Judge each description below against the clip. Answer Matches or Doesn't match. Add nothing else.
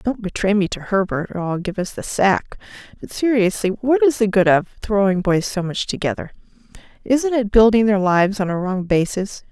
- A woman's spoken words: Matches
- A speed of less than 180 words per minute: Doesn't match